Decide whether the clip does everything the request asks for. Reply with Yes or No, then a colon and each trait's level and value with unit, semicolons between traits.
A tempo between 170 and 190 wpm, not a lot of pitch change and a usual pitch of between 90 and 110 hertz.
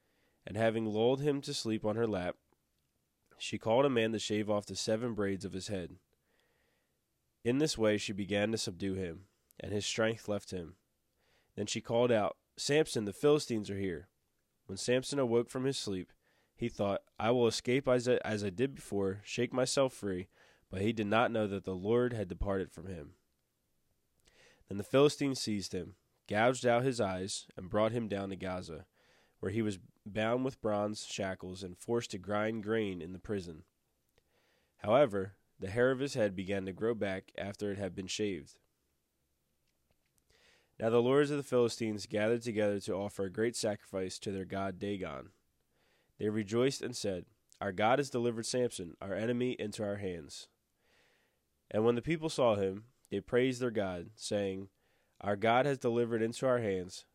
No: average, 180 wpm; average, 3.7 semitones; low, 105 Hz